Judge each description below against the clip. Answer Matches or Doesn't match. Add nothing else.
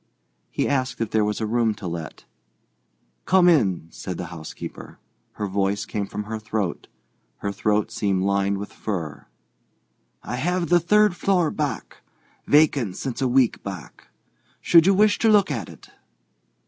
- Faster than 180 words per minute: Doesn't match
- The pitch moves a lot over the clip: Matches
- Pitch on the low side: Matches